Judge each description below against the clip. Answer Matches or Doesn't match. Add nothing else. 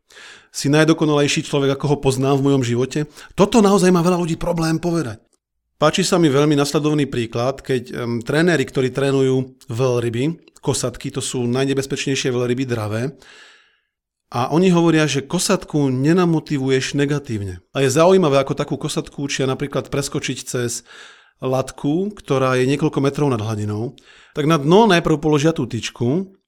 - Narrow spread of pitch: Doesn't match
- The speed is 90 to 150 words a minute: Matches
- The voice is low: Doesn't match